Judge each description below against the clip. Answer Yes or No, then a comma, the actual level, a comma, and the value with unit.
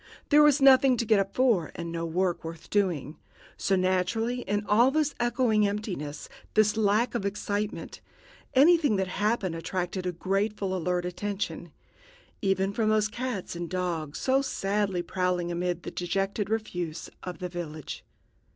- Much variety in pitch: No, average, 3.7 semitones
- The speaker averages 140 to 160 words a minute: Yes, average, 150 wpm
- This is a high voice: Yes, high, 195 Hz